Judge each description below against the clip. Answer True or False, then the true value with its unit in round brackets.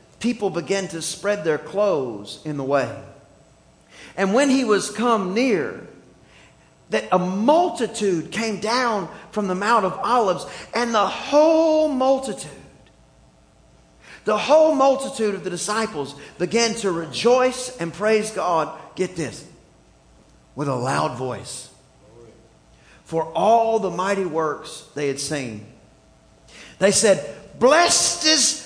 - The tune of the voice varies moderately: False (7.9 semitones)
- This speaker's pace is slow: True (125 wpm)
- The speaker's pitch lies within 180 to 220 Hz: True (190 Hz)